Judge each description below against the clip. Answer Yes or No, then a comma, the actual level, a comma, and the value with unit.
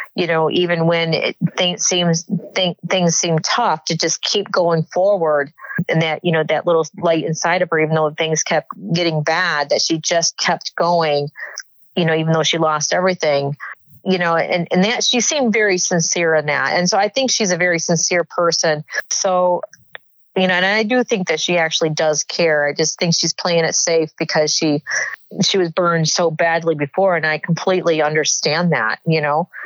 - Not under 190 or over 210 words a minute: Yes, average, 200 wpm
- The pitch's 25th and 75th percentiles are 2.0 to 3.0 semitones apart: Yes, narrow, 2.4 semitones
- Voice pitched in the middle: Yes, medium, 170 Hz